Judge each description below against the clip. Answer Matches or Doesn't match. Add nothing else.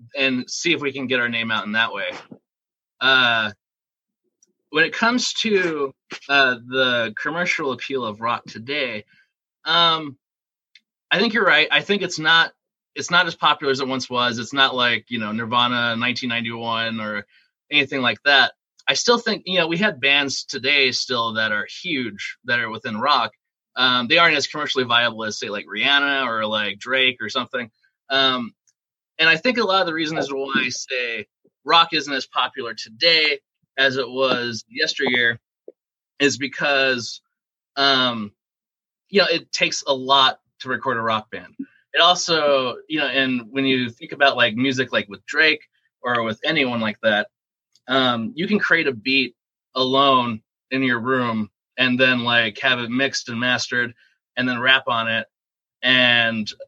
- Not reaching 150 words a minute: Doesn't match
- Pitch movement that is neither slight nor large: Matches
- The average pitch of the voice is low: Matches